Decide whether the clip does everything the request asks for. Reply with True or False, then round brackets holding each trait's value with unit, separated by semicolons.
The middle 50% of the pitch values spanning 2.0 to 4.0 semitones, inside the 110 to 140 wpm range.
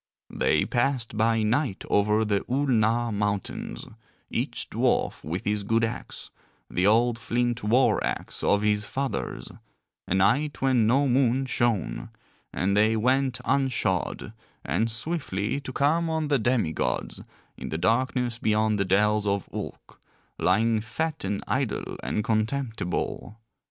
True (3.7 semitones; 135 wpm)